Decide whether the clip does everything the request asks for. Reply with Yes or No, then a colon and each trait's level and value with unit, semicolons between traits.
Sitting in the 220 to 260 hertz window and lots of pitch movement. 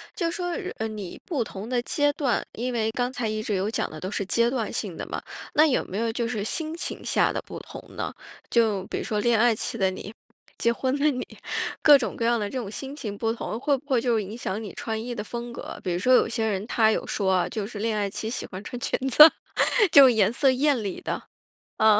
No: high, 230 Hz; average, 3.3 semitones